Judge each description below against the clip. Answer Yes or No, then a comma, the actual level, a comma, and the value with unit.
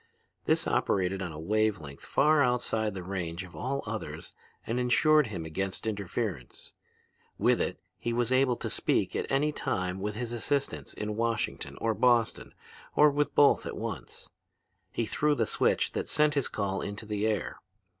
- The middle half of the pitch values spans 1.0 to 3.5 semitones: No, average, 4.6 semitones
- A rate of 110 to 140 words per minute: No, average, 170 wpm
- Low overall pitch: Yes, low, 110 Hz